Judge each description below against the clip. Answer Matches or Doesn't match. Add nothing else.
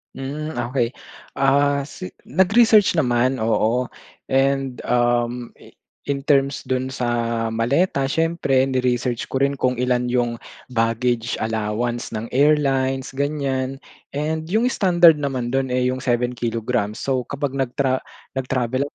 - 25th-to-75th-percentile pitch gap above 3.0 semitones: Doesn't match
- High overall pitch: Doesn't match